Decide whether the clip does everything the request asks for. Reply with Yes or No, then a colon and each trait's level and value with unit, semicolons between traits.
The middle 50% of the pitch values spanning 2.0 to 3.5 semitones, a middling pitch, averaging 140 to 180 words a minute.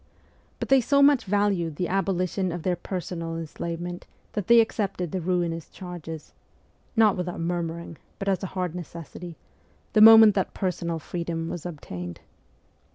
Yes: average, 2.7 semitones; medium, 180 Hz; average, 150 wpm